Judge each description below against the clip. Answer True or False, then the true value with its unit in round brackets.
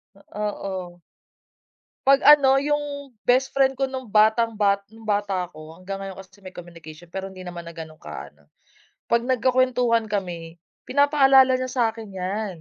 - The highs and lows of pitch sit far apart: True (5.9 semitones)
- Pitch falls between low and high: False (210 Hz)